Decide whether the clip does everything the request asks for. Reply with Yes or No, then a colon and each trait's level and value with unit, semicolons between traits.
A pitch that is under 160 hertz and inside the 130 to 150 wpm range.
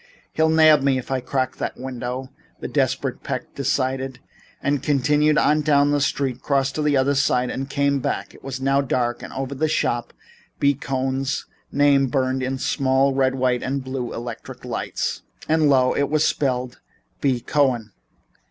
No: low, 135 Hz; average, 175 wpm